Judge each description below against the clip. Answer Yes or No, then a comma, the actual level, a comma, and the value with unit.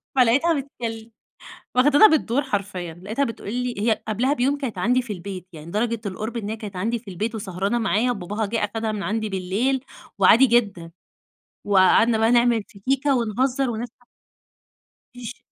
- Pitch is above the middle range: Yes, high, 225 Hz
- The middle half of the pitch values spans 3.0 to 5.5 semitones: Yes, average, 3.5 semitones